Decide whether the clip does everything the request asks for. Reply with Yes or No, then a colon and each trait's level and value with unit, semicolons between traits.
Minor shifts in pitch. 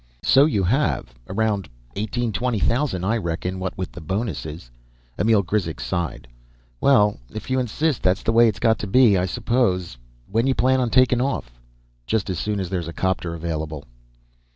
No: average, 5.1 semitones